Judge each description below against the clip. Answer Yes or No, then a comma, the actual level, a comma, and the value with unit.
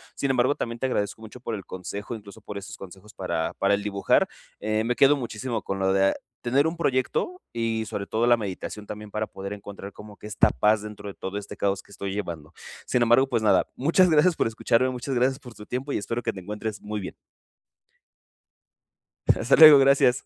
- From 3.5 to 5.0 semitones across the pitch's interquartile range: Yes, average, 3.8 semitones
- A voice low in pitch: Yes, low, 110 Hz